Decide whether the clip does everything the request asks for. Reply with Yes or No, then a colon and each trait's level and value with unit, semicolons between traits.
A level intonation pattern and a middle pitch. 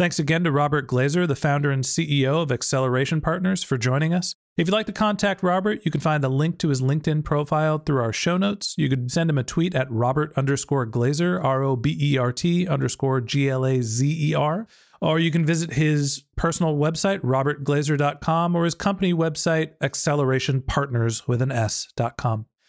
No: average, 3.9 semitones; medium, 150 Hz